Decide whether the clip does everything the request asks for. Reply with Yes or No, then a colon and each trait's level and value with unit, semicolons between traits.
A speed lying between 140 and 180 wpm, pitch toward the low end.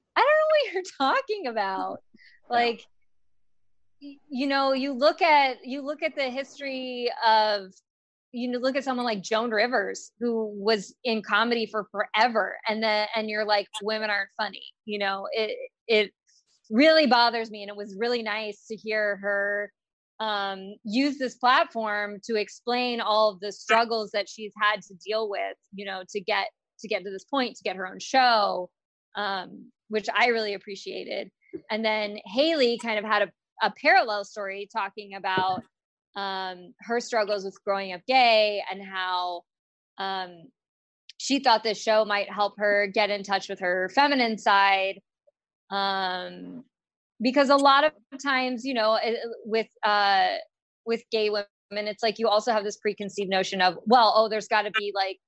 No: average, 170 wpm; high, 215 Hz